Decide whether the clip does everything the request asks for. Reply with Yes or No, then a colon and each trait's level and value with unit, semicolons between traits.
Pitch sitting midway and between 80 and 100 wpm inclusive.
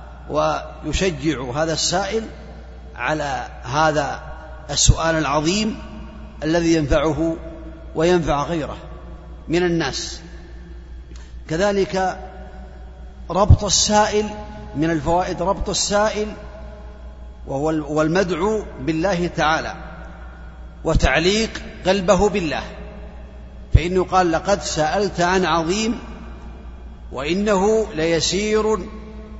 No: medium, 160 Hz; average, 70 wpm